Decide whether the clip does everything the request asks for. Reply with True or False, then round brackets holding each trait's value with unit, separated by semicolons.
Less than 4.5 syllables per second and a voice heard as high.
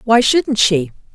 True (3.6 syllables/s; 210 Hz)